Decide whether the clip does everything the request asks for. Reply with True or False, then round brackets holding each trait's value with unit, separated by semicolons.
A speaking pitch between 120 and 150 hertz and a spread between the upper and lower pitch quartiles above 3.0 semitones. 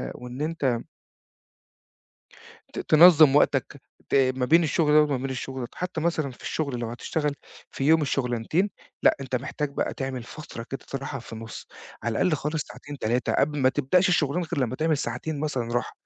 True (140 Hz; 3.7 semitones)